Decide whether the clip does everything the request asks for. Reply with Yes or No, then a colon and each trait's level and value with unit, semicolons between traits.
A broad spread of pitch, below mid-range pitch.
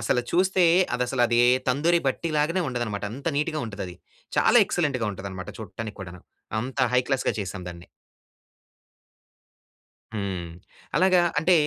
Yes: wide, 7.5 semitones; low, 125 Hz